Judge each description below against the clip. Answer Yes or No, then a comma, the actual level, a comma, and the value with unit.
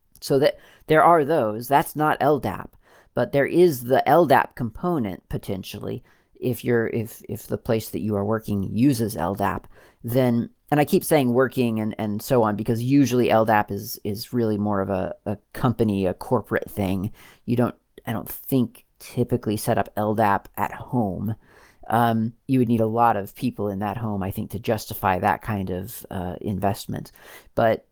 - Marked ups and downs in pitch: No, average, 3.2 semitones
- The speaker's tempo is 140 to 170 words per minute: No, average, 180 wpm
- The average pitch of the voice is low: Yes, low, 110 Hz